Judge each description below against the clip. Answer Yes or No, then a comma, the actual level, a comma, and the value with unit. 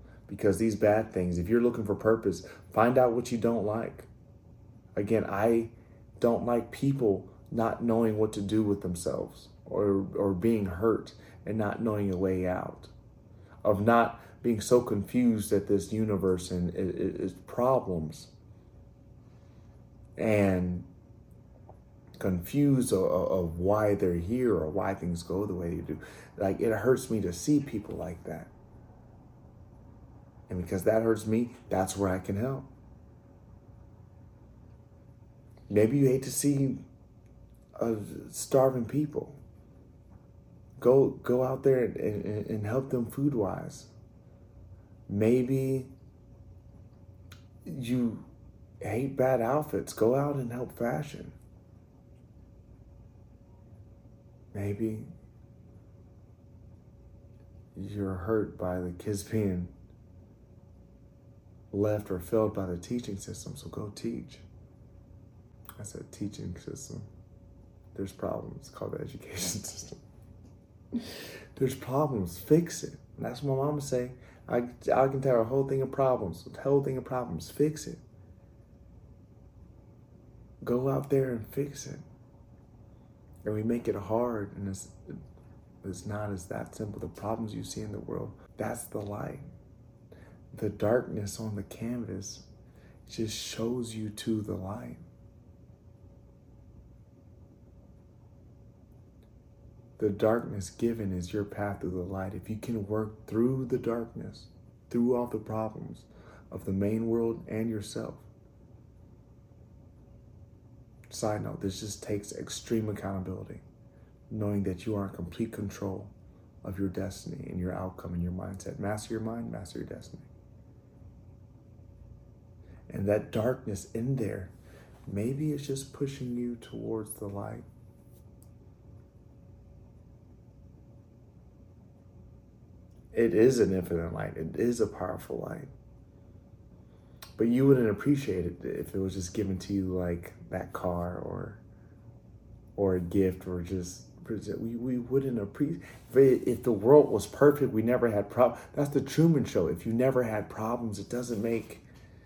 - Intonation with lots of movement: No, average, 3.4 semitones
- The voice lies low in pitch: Yes, low, 110 Hz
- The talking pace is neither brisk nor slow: No, slow, 130 wpm